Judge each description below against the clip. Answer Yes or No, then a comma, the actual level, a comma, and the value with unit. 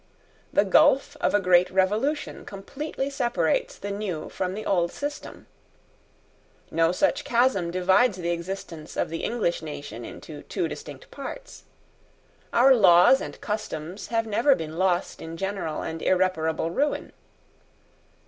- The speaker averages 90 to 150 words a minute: Yes, slow, 135 wpm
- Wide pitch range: Yes, wide, 5.9 semitones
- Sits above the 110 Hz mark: Yes, high, 190 Hz